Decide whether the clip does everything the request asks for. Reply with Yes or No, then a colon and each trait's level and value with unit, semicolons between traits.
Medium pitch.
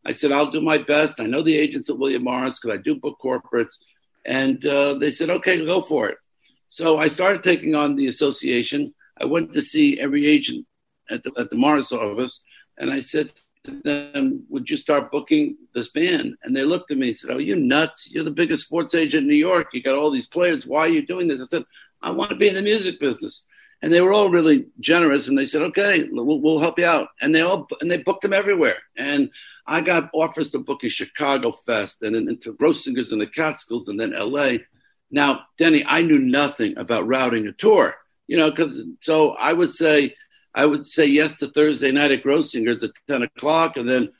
Yes: medium, 165 Hz